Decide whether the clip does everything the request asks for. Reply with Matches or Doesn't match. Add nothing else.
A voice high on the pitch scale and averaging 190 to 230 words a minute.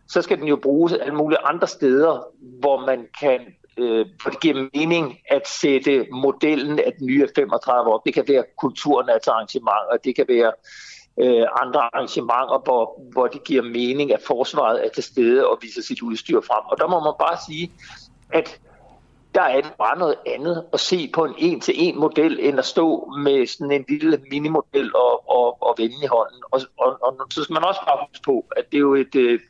Doesn't match